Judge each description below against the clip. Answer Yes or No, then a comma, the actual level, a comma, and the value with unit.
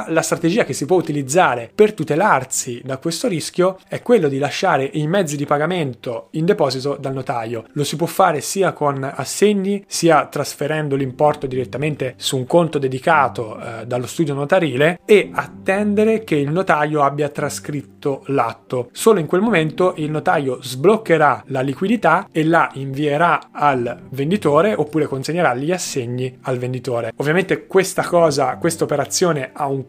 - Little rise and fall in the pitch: No, average, 4.1 semitones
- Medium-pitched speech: Yes, medium, 150 Hz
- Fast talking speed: No, average, 155 wpm